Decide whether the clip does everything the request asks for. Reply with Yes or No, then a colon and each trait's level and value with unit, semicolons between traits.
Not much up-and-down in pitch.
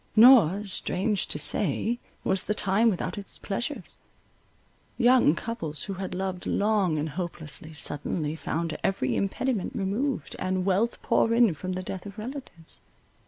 No: average, 4.3 semitones